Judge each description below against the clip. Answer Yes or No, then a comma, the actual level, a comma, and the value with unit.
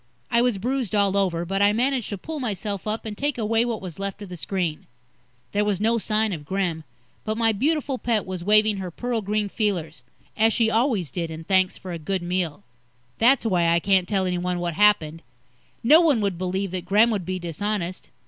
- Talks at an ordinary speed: No, fast, 210 wpm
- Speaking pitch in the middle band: No, high, 200 Hz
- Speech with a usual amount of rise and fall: Yes, average, 3.7 semitones